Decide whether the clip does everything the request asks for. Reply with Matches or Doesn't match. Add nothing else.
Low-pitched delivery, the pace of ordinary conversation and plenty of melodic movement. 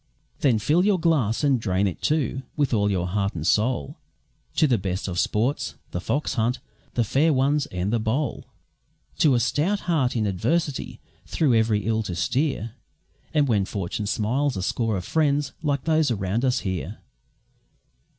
Matches